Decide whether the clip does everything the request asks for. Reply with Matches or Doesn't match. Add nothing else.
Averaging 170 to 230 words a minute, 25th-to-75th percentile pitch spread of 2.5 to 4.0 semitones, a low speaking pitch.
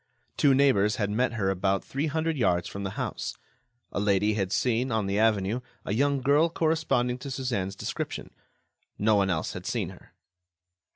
Doesn't match